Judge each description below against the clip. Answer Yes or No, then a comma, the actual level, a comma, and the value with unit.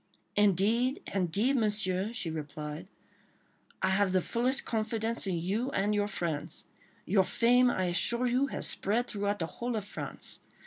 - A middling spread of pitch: Yes, average, 4.2 semitones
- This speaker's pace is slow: No, average, 160 wpm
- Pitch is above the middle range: Yes, high, 205 Hz